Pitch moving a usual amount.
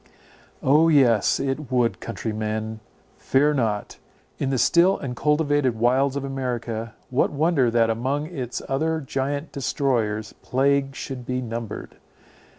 Yes: average, 3.4 semitones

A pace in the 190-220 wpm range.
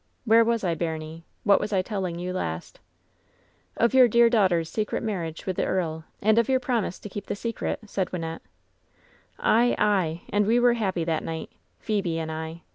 Yes: average, 195 wpm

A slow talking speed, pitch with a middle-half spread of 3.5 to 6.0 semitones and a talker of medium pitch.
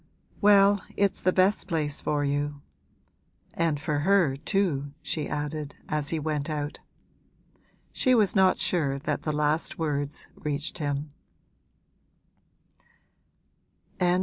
Yes: slow, 115 wpm; average, 4.0 semitones; medium, 150 Hz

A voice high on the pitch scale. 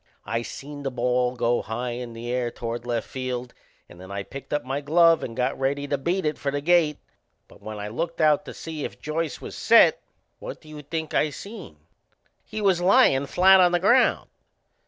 No: medium, 140 Hz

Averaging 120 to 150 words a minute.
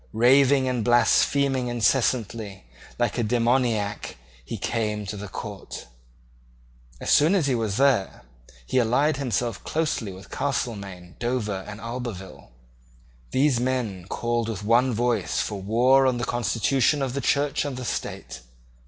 Yes: average, 140 wpm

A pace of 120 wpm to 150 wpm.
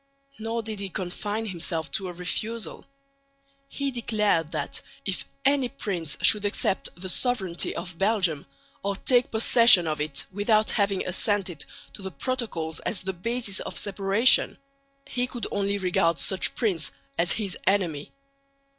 Yes: average, 145 wpm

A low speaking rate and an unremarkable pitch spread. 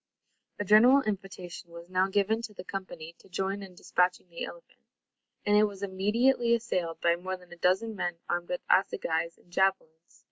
No: average, 180 wpm; average, 3.1 semitones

